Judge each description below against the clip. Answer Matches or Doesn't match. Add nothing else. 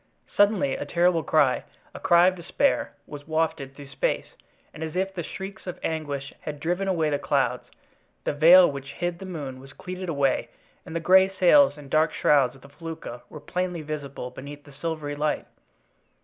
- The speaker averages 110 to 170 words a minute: Doesn't match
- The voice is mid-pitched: Matches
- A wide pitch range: Doesn't match